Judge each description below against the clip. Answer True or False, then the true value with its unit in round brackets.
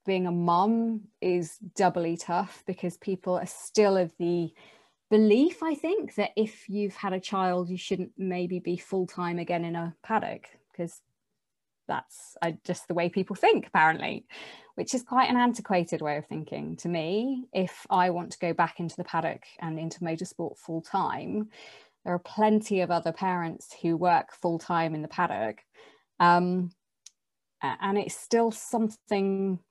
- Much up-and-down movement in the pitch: False (3.2 semitones)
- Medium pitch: True (180 Hz)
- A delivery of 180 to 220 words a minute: False (165 wpm)